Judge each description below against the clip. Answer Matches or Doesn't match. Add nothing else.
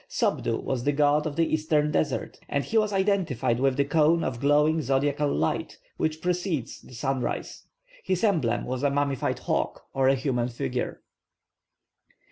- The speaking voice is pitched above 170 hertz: Doesn't match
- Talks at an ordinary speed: Matches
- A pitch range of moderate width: Matches